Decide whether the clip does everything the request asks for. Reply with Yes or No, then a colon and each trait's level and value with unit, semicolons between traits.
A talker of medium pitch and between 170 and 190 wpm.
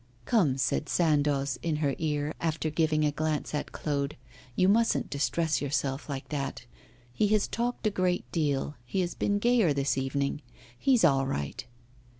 No: medium, 150 Hz; average, 160 wpm